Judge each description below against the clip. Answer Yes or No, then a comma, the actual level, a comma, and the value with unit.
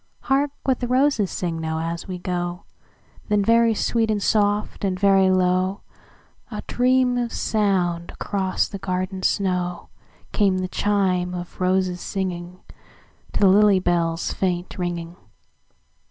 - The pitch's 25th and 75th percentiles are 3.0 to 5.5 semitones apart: No, narrow, 2.6 semitones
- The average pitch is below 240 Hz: Yes, medium, 185 Hz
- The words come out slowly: Yes, slow, 125 wpm